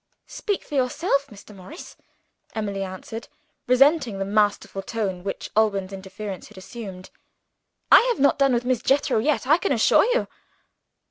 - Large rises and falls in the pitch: Yes, wide, 5.9 semitones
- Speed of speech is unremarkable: Yes, average, 150 wpm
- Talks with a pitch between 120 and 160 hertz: No, high, 225 Hz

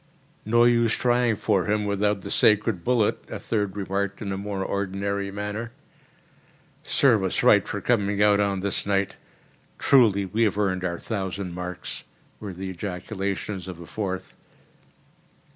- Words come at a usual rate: Yes, average, 150 wpm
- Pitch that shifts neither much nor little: No, narrow, 1.9 semitones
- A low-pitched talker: Yes, low, 100 Hz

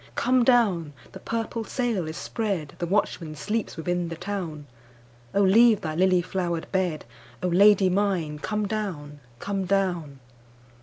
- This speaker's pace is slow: Yes, slow, 125 wpm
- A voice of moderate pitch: Yes, medium, 180 Hz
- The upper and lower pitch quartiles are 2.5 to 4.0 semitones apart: No, average, 4.9 semitones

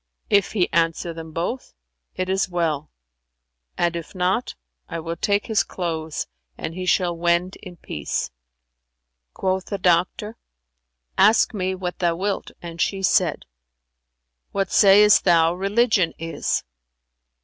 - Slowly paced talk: Yes, slow, 130 wpm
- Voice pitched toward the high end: No, medium, 180 Hz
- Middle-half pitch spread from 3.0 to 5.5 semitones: No, narrow, 2.6 semitones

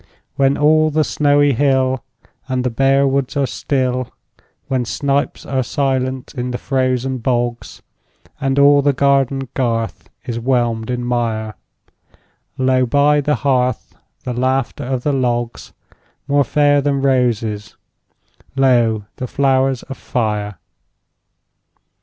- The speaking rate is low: Yes, slow, 125 wpm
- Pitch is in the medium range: No, low, 130 Hz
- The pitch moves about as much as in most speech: No, narrow, 2.2 semitones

